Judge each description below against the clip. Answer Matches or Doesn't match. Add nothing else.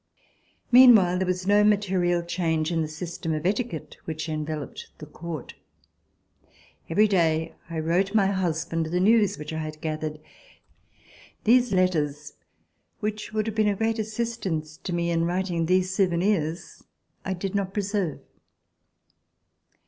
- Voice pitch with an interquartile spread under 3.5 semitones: Doesn't match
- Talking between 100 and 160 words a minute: Matches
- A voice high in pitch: Doesn't match